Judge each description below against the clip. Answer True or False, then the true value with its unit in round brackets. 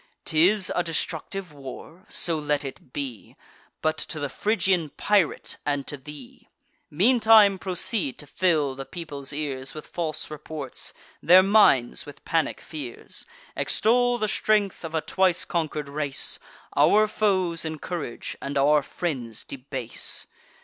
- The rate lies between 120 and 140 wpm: True (135 wpm)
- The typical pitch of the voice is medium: True (155 Hz)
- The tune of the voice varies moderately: True (4.8 semitones)